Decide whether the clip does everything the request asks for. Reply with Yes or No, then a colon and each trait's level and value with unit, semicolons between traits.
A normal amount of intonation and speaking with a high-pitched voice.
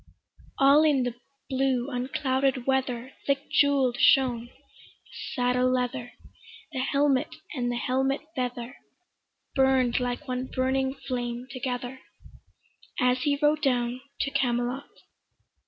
No: narrow, 1.6 semitones; very high, 255 Hz